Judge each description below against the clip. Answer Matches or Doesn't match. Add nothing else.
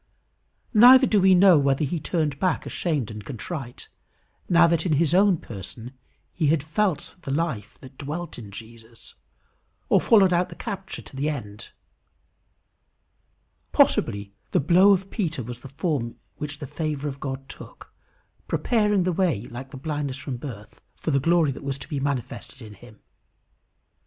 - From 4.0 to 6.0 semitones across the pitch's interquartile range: Matches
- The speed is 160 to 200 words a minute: Matches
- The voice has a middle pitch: Matches